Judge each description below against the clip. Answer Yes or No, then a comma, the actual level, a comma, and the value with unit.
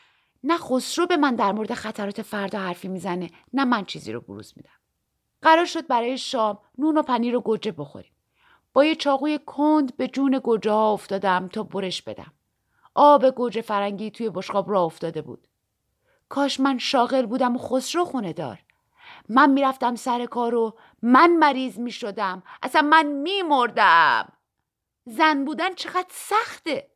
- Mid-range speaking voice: No, very high, 250 Hz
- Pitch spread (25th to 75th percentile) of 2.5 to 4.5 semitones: No, wide, 5.6 semitones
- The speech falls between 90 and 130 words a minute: No, average, 150 wpm